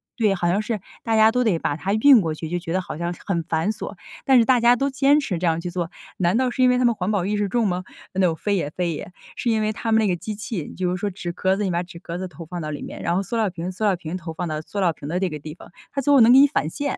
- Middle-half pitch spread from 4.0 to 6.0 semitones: Yes, average, 4.5 semitones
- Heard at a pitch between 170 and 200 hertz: Yes, high, 190 Hz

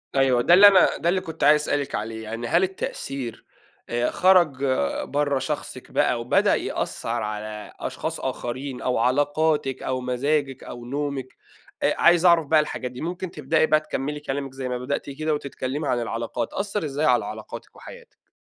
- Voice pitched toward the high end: No, medium, 140 Hz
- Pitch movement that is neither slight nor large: Yes, average, 3.8 semitones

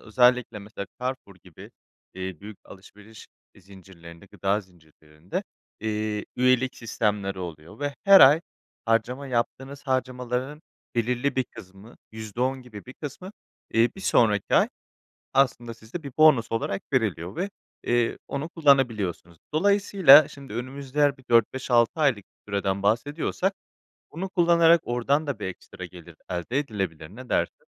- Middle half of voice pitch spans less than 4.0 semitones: No, wide, 5.6 semitones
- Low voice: Yes, low, 120 Hz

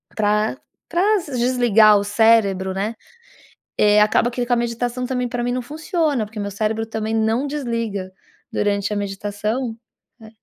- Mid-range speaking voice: No, high, 225 Hz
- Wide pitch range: No, average, 2.9 semitones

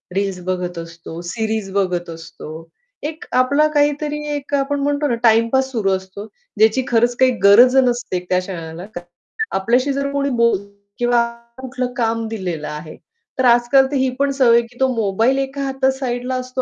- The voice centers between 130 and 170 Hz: No, high, 240 Hz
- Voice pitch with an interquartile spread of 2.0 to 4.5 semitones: No, wide, 5.6 semitones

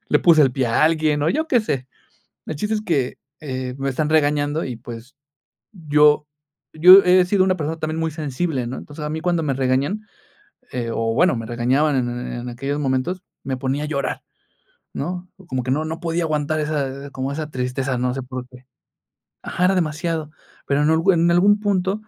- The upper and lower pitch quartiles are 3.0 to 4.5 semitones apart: Yes, average, 4.2 semitones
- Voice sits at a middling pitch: Yes, medium, 150 Hz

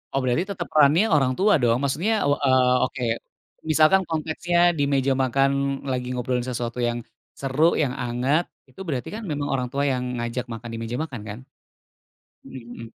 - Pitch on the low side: Yes, low, 130 Hz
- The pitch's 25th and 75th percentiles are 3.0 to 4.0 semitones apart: Yes, average, 3.6 semitones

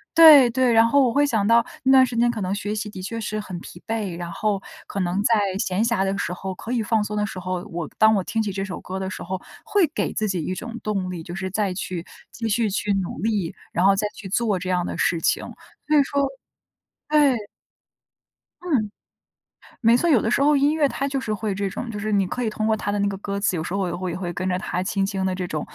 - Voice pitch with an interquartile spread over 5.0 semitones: No, average, 3.8 semitones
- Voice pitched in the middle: No, high, 205 Hz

